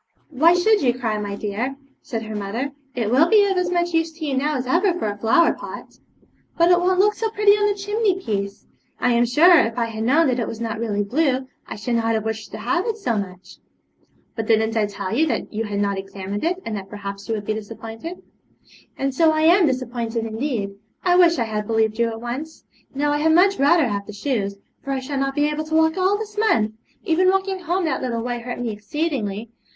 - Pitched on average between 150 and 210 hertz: No, very high, 255 Hz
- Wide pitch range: Yes, wide, 7.4 semitones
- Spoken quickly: Yes, fast, 240 wpm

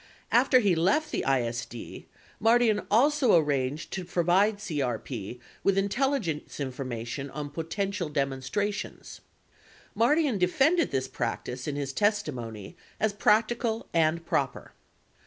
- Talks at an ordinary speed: No, slow, 120 wpm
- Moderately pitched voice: Yes, medium, 175 Hz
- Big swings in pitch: Yes, wide, 8.1 semitones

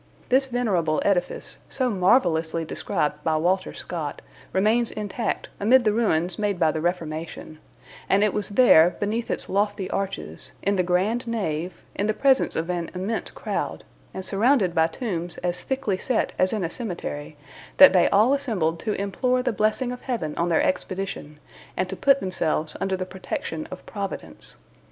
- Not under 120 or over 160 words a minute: No, average, 170 wpm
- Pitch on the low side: No, high, 190 Hz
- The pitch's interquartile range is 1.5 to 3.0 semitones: No, average, 4.8 semitones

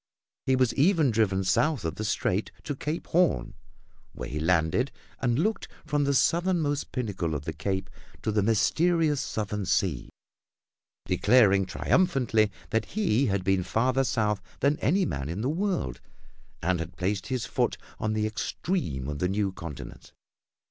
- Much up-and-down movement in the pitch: Yes, wide, 7.1 semitones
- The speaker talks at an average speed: Yes, average, 155 wpm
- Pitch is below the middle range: Yes, low, 110 Hz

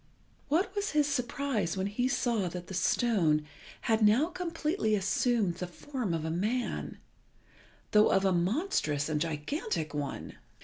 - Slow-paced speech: No, average, 145 wpm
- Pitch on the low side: No, high, 210 Hz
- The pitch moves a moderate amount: No, wide, 8.0 semitones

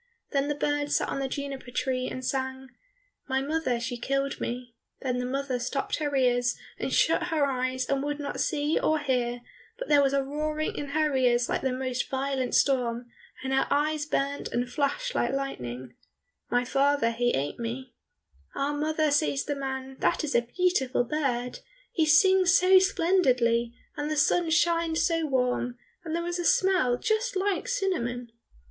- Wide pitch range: No, average, 3.6 semitones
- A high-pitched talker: Yes, very high, 275 Hz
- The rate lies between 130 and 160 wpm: No, average, 180 wpm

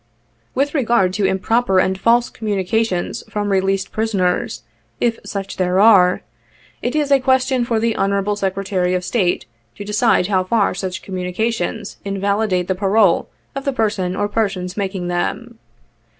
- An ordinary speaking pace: Yes, average, 150 wpm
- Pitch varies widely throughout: No, average, 3.4 semitones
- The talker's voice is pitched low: No, high, 200 Hz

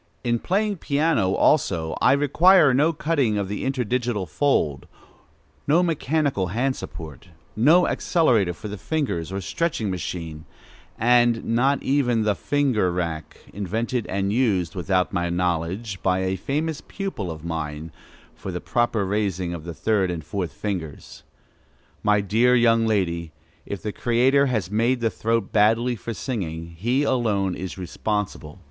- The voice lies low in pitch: Yes, low, 105 Hz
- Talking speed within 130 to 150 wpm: Yes, average, 145 wpm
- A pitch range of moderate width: No, wide, 5.9 semitones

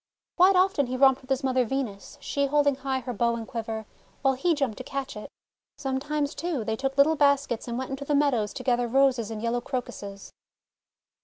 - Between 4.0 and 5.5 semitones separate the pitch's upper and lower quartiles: No, average, 3.1 semitones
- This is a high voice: Yes, very high, 265 Hz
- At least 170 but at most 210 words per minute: Yes, fast, 205 wpm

